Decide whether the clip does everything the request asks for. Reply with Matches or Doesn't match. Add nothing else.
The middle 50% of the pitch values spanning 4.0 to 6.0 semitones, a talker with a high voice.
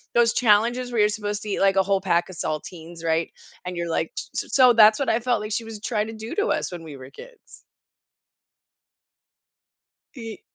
Matches